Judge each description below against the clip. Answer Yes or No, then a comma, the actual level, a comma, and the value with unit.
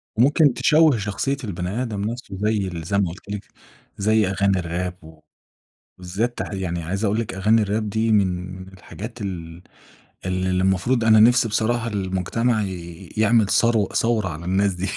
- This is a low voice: Yes, low, 100 Hz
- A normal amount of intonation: Yes, average, 3.5 semitones